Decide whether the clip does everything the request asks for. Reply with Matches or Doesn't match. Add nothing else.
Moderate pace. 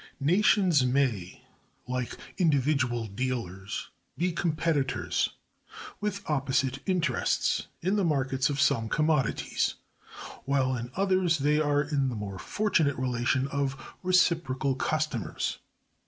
Doesn't match